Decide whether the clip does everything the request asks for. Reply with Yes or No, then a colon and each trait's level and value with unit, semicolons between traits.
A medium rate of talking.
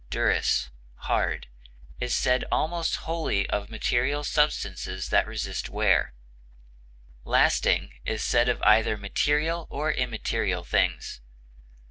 No: slow, 105 wpm